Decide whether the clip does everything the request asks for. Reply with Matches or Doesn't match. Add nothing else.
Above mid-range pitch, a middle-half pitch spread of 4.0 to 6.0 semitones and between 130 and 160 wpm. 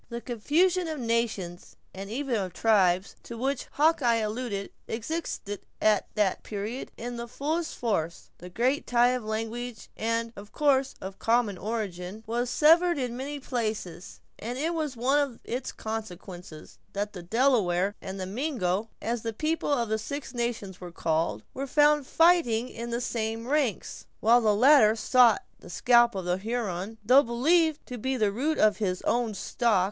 Doesn't match